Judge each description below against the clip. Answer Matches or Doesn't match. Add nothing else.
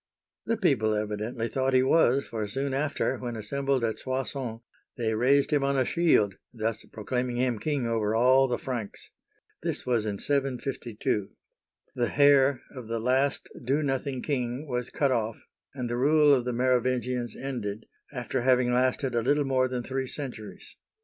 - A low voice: Matches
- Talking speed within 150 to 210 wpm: Matches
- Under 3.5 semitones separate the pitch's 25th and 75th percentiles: Matches